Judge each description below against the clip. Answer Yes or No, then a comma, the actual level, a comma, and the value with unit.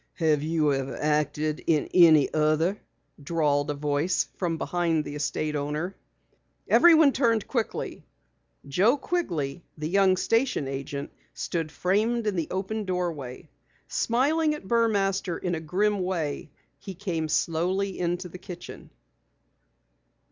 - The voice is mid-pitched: Yes, medium, 175 Hz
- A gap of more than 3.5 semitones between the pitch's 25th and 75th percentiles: Yes, average, 4.6 semitones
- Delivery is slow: Yes, slow, 125 wpm